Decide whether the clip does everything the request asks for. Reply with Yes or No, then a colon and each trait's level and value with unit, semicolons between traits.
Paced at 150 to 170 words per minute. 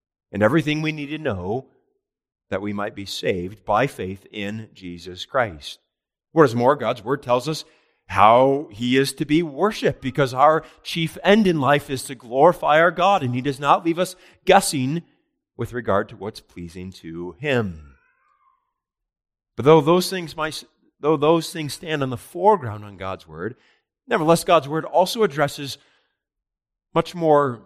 Yes: average, 165 wpm